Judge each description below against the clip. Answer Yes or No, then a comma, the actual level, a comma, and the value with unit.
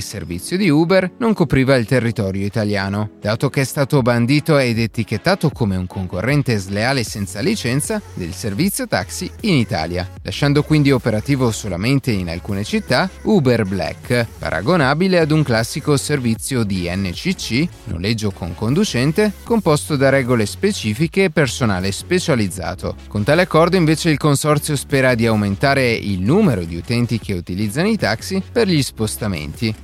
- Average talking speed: Yes, average, 145 wpm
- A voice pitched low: Yes, low, 120 Hz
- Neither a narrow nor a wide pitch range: No, wide, 6.8 semitones